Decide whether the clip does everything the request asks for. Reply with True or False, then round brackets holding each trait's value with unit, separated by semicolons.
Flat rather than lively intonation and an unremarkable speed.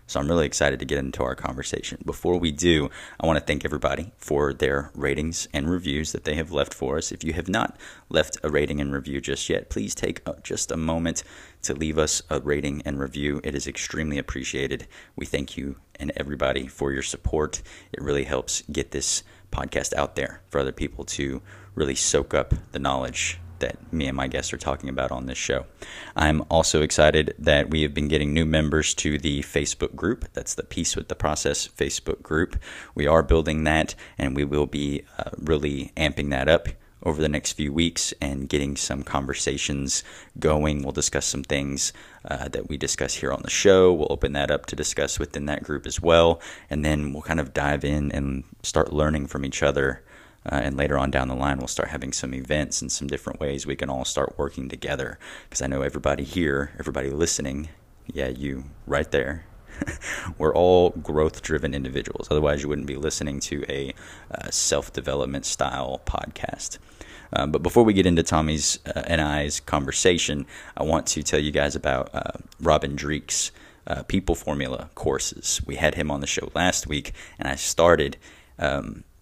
True (2.1 semitones; 195 wpm)